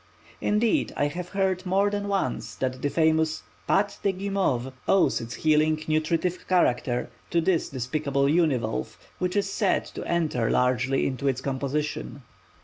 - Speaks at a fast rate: No, average, 145 wpm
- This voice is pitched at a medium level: Yes, medium, 155 Hz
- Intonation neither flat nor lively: No, wide, 5.7 semitones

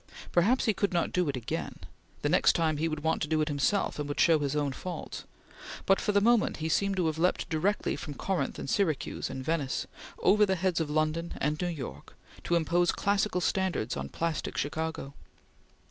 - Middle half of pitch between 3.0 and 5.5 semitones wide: Yes, average, 3.9 semitones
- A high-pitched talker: No, medium, 165 Hz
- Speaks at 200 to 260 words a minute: Yes, fast, 205 wpm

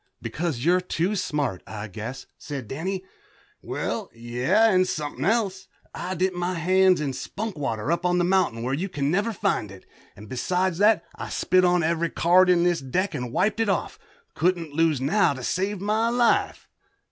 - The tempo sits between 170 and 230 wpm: Yes, average, 180 wpm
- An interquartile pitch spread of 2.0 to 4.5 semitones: No, average, 5.1 semitones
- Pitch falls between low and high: Yes, medium, 175 Hz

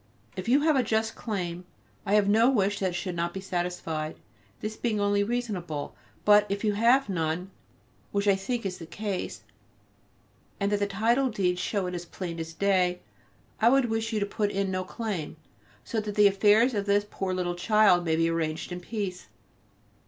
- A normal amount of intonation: Yes, average, 3.3 semitones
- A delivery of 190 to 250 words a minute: Yes, average, 195 wpm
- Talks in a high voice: Yes, high, 200 Hz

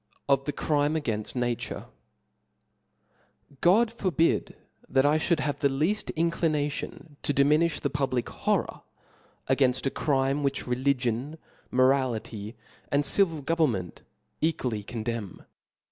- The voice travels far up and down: No, average, 3.7 semitones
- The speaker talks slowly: Yes, slow, 130 wpm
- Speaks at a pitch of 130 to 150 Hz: Yes, medium, 140 Hz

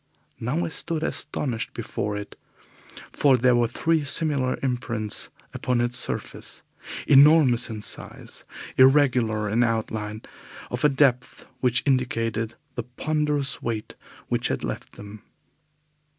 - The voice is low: Yes, low, 125 Hz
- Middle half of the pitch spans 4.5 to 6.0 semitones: No, average, 3.8 semitones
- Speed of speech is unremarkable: No, slow, 120 wpm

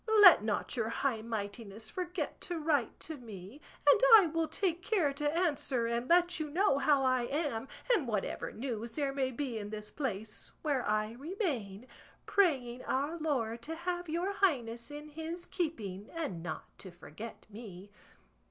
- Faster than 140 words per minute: Yes, average, 165 wpm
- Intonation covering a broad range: Yes, wide, 6.5 semitones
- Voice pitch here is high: Yes, very high, 275 Hz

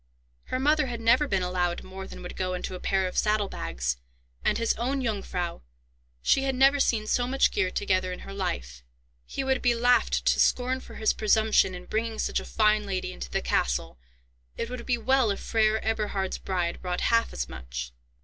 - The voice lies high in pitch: Yes, high, 205 Hz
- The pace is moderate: Yes, average, 195 wpm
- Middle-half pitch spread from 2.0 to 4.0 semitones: No, average, 5.0 semitones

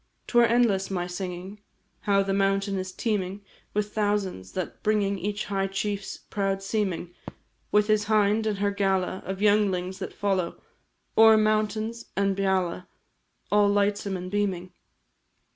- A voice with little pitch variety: Yes, narrow, 1.7 semitones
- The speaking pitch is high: Yes, high, 200 Hz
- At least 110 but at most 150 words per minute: Yes, average, 145 wpm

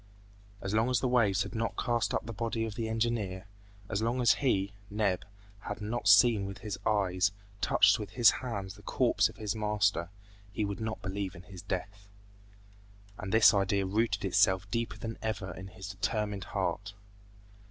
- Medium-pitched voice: No, low, 105 Hz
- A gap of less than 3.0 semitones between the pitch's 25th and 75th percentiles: Yes, narrow, 2.6 semitones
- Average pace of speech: Yes, average, 180 wpm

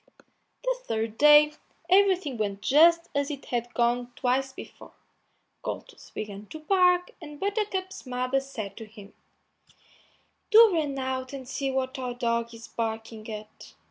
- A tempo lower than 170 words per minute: Yes, average, 140 wpm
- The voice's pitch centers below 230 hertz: No, very high, 260 Hz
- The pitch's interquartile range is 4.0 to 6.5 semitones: Yes, average, 5.1 semitones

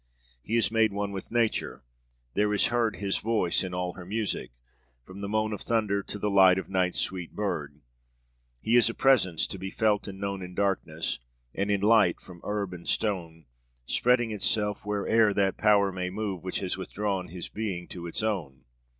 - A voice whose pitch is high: No, low, 100 Hz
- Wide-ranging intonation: No, average, 2.7 semitones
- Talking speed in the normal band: Yes, average, 190 wpm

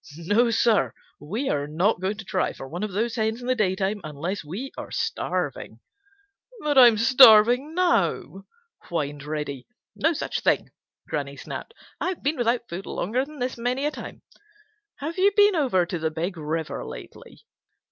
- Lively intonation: Yes, wide, 7.2 semitones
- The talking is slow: No, average, 165 wpm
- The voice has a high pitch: Yes, high, 215 Hz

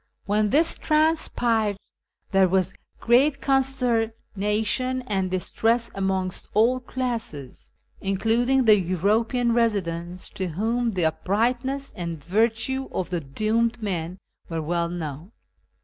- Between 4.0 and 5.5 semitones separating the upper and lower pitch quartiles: Yes, average, 4.8 semitones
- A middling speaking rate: No, slow, 110 wpm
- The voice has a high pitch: Yes, high, 215 Hz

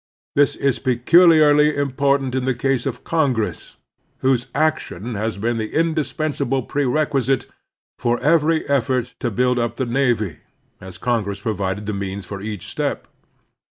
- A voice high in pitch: No, low, 125 Hz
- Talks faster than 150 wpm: No, average, 145 wpm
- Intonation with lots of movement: No, average, 4.3 semitones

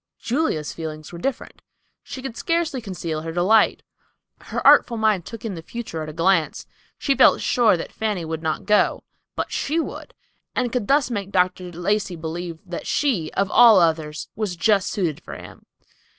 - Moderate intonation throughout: No, wide, 5.7 semitones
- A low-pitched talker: No, high, 190 Hz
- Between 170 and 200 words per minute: Yes, average, 180 wpm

